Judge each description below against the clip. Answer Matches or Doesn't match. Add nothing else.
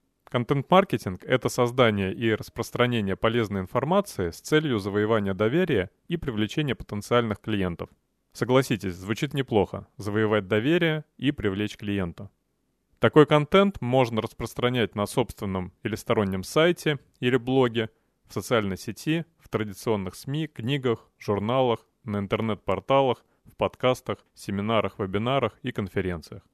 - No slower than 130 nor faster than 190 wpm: Doesn't match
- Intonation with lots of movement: Doesn't match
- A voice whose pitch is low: Matches